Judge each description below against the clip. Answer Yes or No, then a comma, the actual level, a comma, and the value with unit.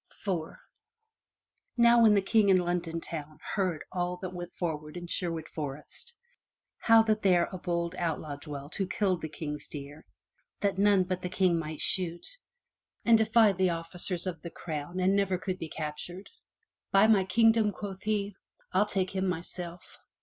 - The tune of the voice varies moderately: Yes, average, 3.2 semitones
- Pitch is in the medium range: Yes, medium, 180 Hz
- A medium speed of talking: Yes, average, 165 wpm